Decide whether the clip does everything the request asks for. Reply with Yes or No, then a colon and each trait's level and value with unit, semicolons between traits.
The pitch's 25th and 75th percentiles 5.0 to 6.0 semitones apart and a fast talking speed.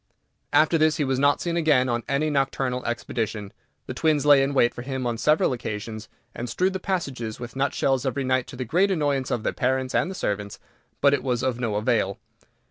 No: average, 3.4 semitones; fast, 215 wpm